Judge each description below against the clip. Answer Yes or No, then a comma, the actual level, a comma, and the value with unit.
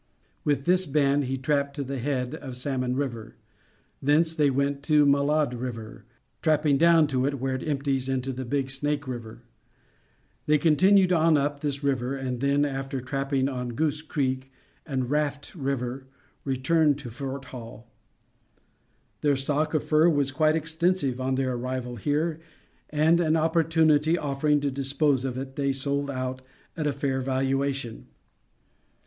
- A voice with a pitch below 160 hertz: Yes, medium, 140 Hz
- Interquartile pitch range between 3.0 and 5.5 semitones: No, narrow, 2.4 semitones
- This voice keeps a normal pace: Yes, average, 155 wpm